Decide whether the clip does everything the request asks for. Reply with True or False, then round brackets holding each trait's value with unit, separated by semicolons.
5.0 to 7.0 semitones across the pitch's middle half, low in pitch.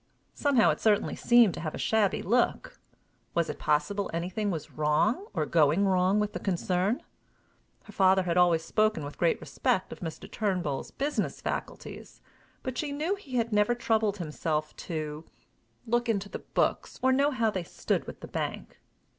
False (5.4 semitones; 195 Hz)